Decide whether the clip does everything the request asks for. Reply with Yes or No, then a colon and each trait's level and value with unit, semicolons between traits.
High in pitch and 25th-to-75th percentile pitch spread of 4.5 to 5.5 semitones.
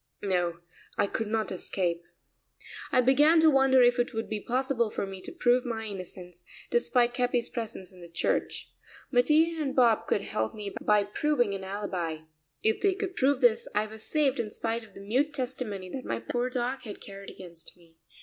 Yes: high, 225 Hz; average, 4.8 semitones